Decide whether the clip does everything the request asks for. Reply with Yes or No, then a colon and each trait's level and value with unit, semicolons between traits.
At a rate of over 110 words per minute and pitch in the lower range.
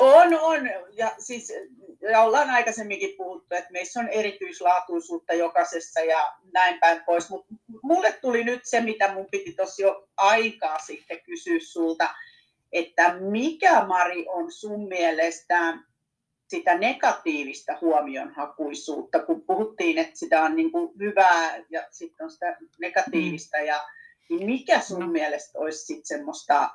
No: average, 135 wpm; high, 195 Hz